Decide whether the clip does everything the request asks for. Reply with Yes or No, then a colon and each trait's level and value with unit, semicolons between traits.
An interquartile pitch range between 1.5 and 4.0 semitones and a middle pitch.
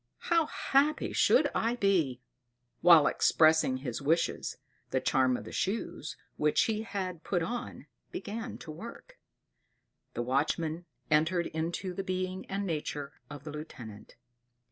No: average, 4.9 semitones; medium, 170 Hz